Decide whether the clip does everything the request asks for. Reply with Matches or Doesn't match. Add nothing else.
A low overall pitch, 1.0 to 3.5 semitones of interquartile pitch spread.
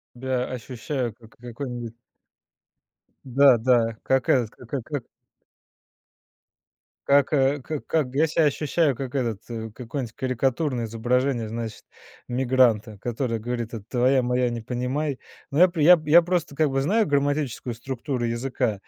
Matches